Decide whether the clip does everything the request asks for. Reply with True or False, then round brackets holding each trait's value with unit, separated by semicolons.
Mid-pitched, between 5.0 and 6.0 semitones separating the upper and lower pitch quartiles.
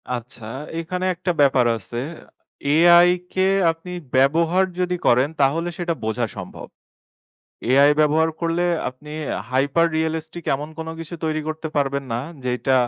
False (155 Hz; 3.9 semitones)